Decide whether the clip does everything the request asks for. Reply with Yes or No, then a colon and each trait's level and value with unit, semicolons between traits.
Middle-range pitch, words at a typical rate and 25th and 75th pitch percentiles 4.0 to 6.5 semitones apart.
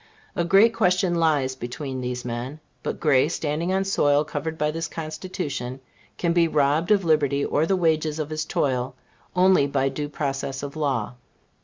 No: medium, 150 Hz; average, 170 wpm; average, 3.6 semitones